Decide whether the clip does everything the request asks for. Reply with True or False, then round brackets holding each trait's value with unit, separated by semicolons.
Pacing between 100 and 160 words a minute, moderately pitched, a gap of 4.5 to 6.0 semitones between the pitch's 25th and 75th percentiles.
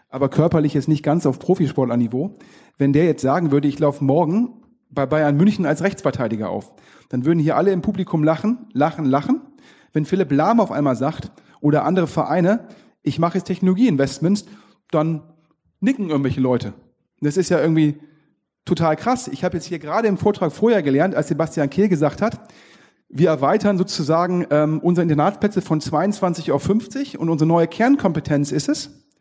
False (175 wpm; 165 Hz; 4.9 semitones)